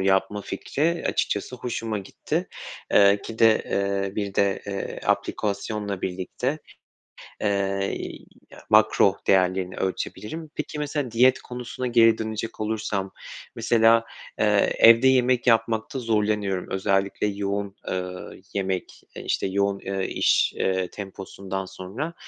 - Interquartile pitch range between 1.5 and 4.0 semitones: Yes, average, 2.9 semitones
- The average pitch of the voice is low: Yes, low, 100 Hz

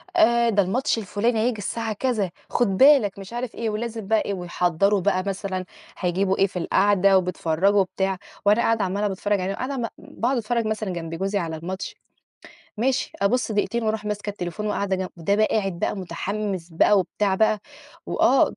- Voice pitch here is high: Yes, high, 205 Hz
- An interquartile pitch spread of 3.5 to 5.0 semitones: No, average, 2.8 semitones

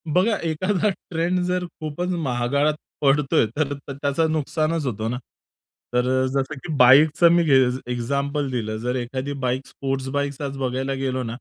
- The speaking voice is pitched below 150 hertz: Yes, medium, 140 Hz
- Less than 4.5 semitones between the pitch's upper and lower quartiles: Yes, average, 3.5 semitones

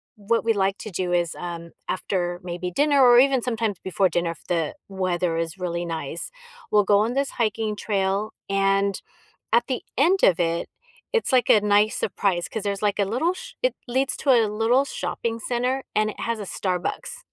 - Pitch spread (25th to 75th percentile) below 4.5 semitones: No, average, 4.8 semitones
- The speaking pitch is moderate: No, high, 205 Hz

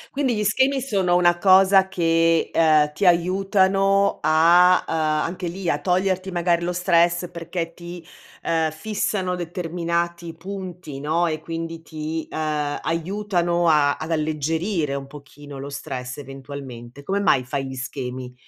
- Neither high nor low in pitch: Yes, medium, 170 Hz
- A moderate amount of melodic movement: Yes, average, 3.1 semitones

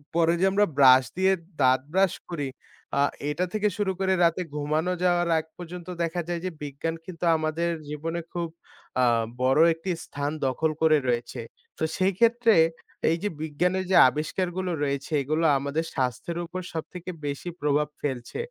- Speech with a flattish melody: No, average, 3.8 semitones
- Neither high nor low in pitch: Yes, medium, 165 Hz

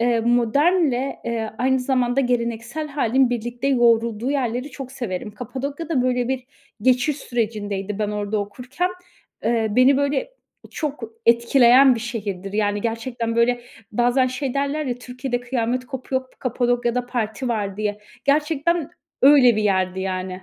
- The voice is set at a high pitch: Yes, high, 245 Hz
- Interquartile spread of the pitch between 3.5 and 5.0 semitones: No, average, 2.9 semitones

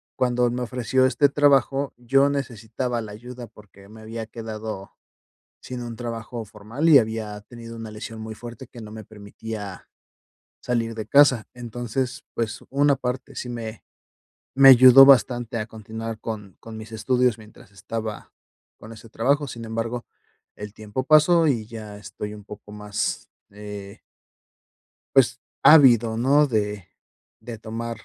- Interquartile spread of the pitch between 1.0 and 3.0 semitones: Yes, narrow, 2.6 semitones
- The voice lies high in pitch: No, low, 115 Hz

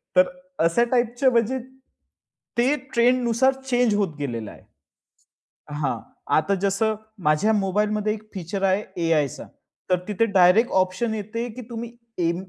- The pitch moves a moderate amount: Yes, average, 4.5 semitones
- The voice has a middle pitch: No, high, 210 Hz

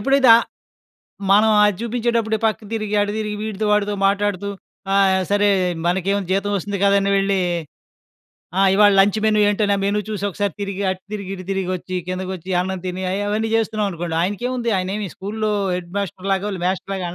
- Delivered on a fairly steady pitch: Yes, narrow, 1.9 semitones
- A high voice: Yes, high, 200 Hz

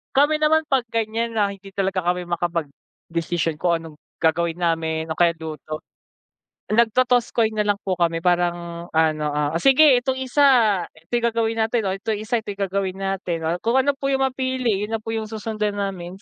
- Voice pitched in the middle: No, high, 200 Hz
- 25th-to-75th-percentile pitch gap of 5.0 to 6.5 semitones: Yes, average, 5.3 semitones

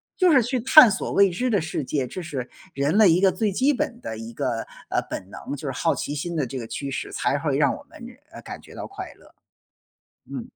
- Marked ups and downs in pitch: Yes, wide, 9.0 semitones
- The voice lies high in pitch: No, medium, 165 Hz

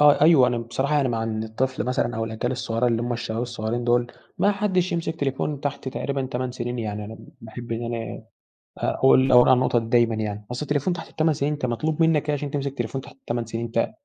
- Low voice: Yes, low, 125 Hz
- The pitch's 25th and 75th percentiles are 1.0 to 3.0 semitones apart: No, average, 3.6 semitones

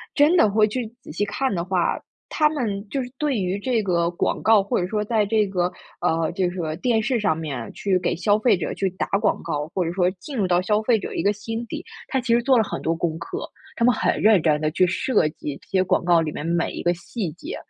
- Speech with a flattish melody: No, average, 4.8 semitones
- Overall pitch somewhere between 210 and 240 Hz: No, high, 195 Hz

